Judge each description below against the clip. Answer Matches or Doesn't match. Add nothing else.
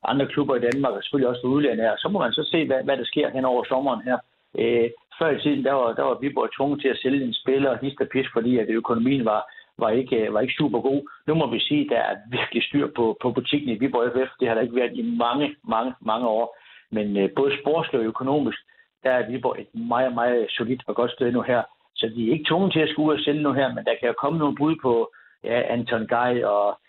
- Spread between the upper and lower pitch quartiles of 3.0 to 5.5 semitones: Matches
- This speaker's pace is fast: Matches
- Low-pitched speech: Matches